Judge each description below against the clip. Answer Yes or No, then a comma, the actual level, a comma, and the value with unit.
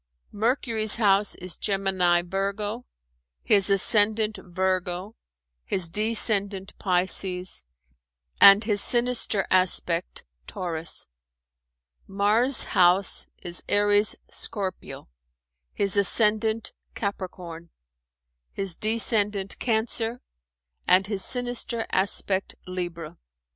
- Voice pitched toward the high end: Yes, high, 200 Hz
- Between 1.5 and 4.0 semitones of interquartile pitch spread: Yes, average, 2.8 semitones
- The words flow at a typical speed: No, slow, 80 wpm